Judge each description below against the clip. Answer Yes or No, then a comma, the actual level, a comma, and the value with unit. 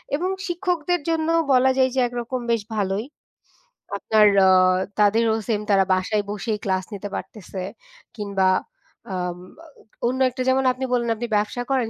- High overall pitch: Yes, high, 230 Hz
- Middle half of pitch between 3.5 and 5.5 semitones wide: Yes, average, 4.2 semitones